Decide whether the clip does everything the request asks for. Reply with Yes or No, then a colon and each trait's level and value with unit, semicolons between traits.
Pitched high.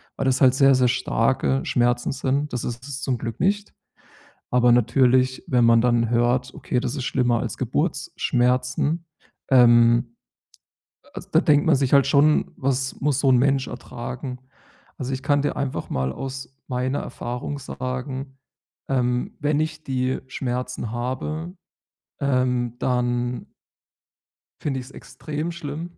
No: low, 130 Hz